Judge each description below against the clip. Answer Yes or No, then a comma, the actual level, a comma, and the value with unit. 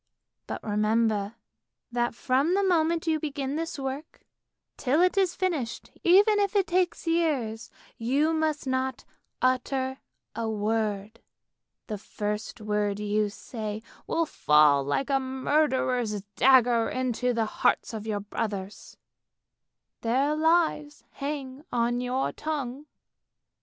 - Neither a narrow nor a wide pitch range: No, wide, 5.7 semitones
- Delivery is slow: Yes, slow, 120 wpm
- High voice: Yes, very high, 255 Hz